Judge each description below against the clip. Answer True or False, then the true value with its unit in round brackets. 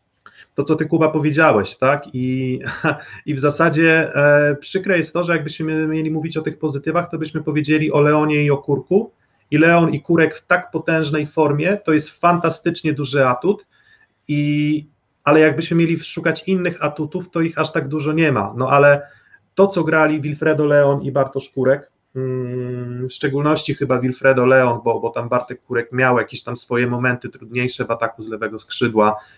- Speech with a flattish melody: False (3.8 semitones)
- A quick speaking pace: True (175 wpm)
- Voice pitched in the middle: True (150 Hz)